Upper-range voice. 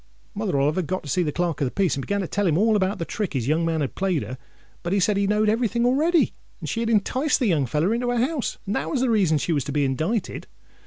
Yes: high, 195 Hz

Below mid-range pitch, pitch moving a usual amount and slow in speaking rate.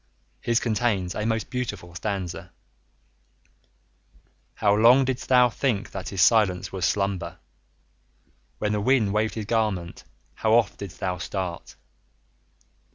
Yes: low, 105 Hz; average, 3.5 semitones; slow, 125 wpm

